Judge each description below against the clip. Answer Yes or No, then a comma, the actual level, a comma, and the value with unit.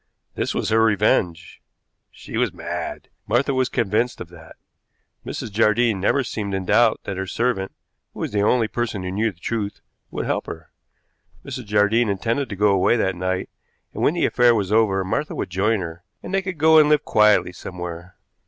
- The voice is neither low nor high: No, low, 105 Hz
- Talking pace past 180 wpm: Yes, average, 190 wpm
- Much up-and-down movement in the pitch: No, average, 3.9 semitones